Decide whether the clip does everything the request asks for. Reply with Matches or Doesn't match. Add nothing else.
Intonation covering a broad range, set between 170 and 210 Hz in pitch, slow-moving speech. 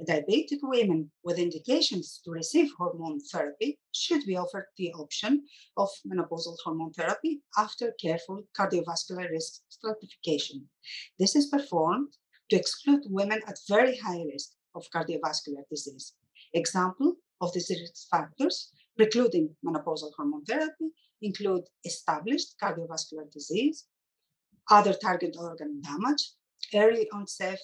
Matches